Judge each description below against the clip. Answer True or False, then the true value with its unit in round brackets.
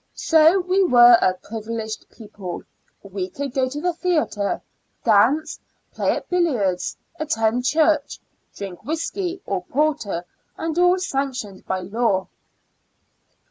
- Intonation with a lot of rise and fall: True (7.8 semitones)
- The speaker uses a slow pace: True (120 wpm)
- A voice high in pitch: True (250 Hz)